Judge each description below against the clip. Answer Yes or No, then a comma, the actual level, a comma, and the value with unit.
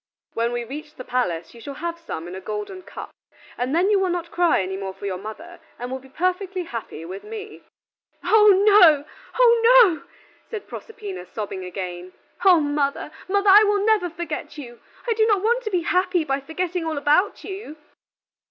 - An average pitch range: No, wide, 8.5 semitones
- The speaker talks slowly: No, average, 190 wpm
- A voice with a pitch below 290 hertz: No, very high, 330 Hz